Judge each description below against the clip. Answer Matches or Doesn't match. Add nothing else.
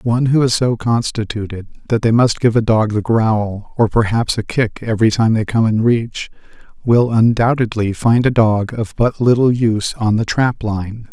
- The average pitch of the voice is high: Doesn't match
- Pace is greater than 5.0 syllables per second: Doesn't match